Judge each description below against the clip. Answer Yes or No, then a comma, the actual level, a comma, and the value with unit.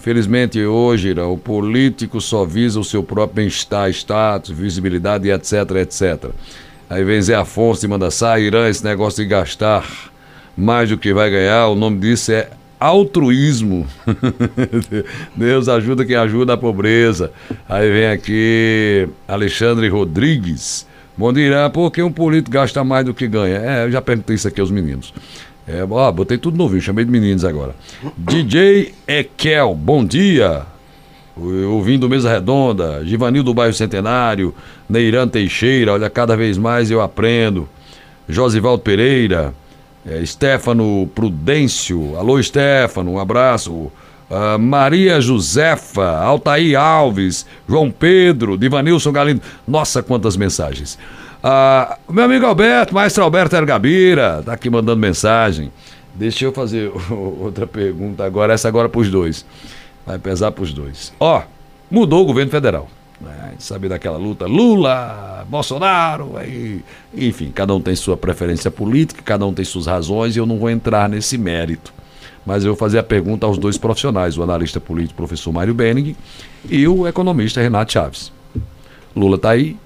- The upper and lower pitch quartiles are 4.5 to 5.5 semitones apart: Yes, average, 4.8 semitones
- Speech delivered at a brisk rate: No, average, 150 wpm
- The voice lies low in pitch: Yes, low, 110 Hz